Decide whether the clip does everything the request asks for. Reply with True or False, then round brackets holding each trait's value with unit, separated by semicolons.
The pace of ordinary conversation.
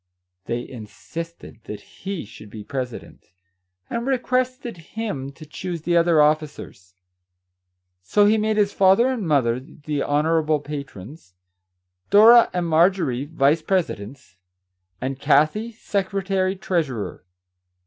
False (120 wpm)